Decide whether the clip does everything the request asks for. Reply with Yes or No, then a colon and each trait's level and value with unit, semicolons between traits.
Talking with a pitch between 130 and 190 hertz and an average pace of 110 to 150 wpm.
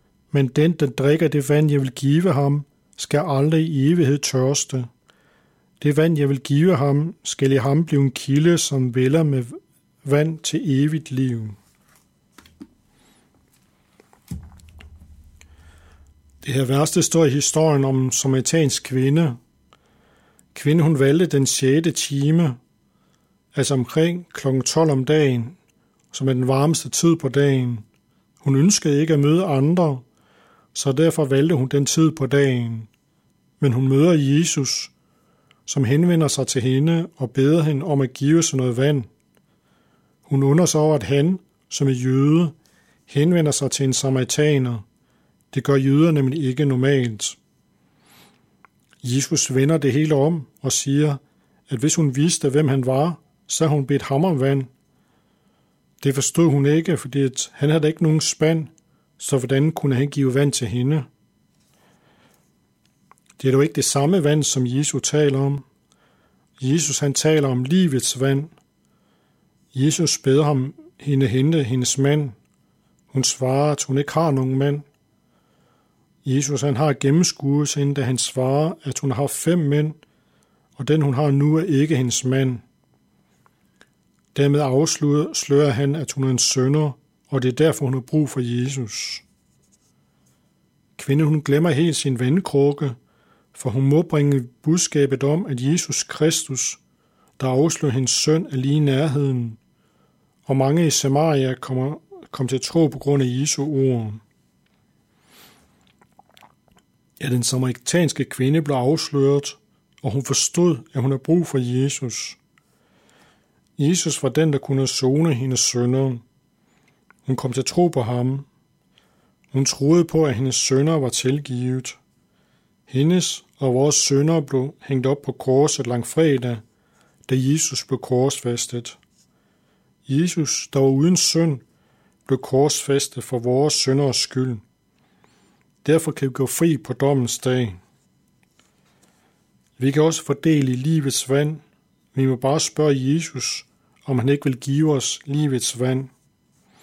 Yes: medium, 140 Hz; slow, 145 wpm